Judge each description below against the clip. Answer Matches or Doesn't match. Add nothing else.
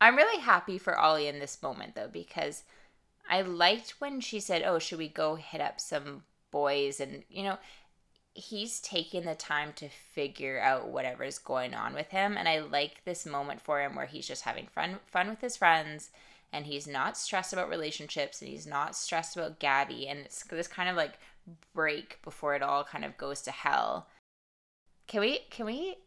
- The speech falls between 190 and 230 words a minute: Matches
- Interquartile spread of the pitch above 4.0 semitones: Matches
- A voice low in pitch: Doesn't match